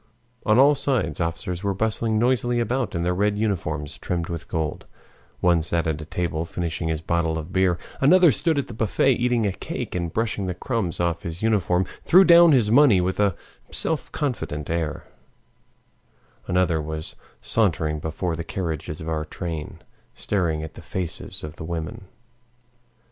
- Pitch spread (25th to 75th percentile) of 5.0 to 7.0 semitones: Yes, wide, 5.5 semitones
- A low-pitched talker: Yes, very low, 90 Hz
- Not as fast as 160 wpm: No, average, 170 wpm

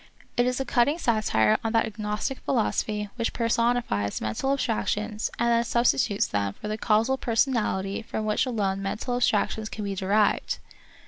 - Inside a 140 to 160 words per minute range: No, average, 170 wpm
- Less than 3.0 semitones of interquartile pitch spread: Yes, narrow, 2.6 semitones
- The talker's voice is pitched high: Yes, high, 220 Hz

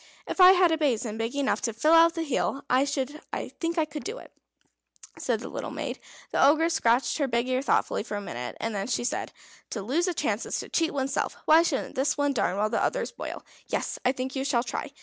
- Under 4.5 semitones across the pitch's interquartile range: No, average, 5.0 semitones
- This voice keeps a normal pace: No, fast, 235 wpm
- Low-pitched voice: No, very high, 275 Hz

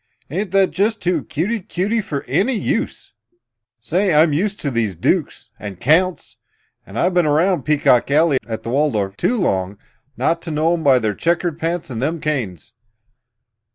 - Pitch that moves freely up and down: Yes, wide, 6.3 semitones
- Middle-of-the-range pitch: Yes, medium, 155 Hz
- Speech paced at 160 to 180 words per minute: Yes, average, 165 wpm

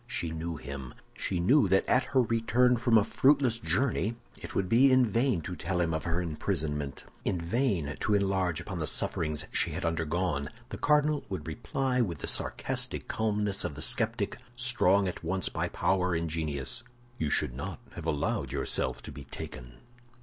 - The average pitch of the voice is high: No, very low, 90 Hz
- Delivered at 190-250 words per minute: No, average, 180 wpm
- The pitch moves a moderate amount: No, wide, 6.7 semitones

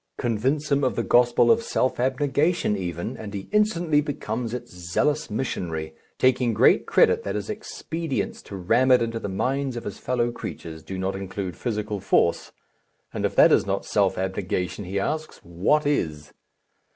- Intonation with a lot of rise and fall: Yes, wide, 6.6 semitones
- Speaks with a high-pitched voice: No, low, 115 Hz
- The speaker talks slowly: No, average, 170 wpm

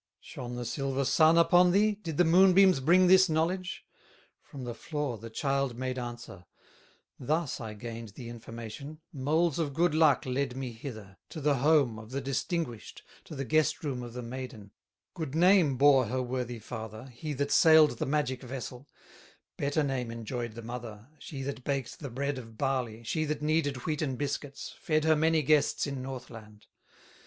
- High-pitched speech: No, low, 135 Hz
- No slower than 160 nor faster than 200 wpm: Yes, average, 175 wpm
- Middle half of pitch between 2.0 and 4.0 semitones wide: No, average, 4.4 semitones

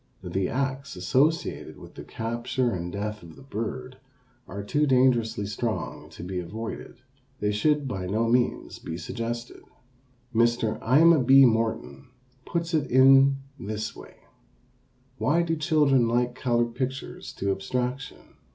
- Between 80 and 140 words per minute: Yes, slow, 135 wpm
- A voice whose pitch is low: Yes, low, 120 Hz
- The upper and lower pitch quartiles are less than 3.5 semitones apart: No, average, 3.8 semitones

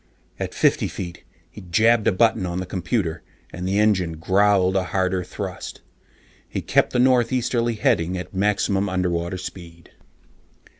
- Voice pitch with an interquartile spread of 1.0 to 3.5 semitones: Yes, average, 2.8 semitones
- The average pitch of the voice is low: Yes, very low, 95 Hz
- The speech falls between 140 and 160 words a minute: Yes, average, 145 wpm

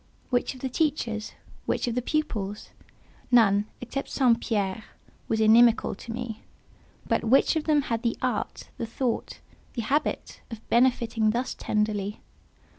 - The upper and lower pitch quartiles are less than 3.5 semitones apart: Yes, average, 2.8 semitones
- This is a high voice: Yes, high, 235 Hz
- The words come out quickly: No, average, 145 wpm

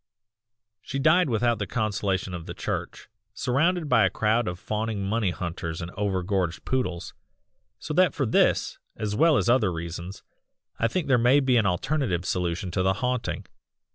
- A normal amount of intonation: No, wide, 5.7 semitones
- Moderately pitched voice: No, low, 105 Hz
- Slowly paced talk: No, average, 170 wpm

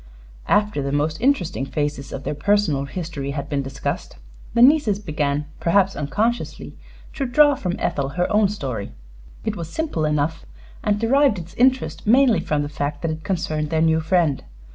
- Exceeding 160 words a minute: Yes, average, 170 wpm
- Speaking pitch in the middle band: Yes, medium, 165 Hz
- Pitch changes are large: Yes, wide, 6.2 semitones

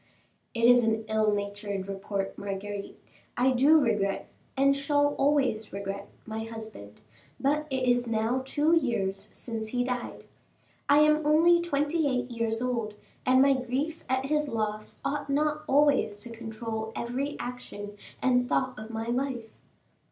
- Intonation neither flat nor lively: Yes, average, 4.3 semitones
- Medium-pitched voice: No, high, 245 Hz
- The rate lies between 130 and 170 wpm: Yes, average, 150 wpm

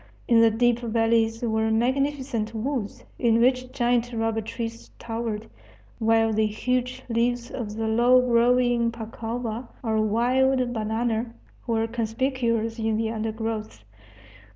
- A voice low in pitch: No, high, 230 Hz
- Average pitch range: No, narrow, 1.5 semitones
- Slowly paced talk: Yes, slow, 125 wpm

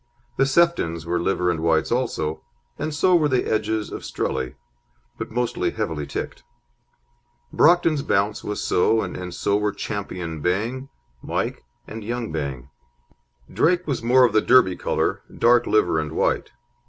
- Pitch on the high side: No, low, 105 Hz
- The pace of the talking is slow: No, average, 150 wpm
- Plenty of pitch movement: Yes, wide, 7.3 semitones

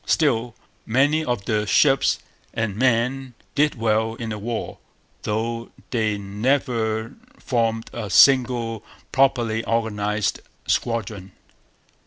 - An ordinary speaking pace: No, slow, 105 wpm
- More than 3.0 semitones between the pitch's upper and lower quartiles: No, narrow, 2.5 semitones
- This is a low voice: Yes, low, 115 Hz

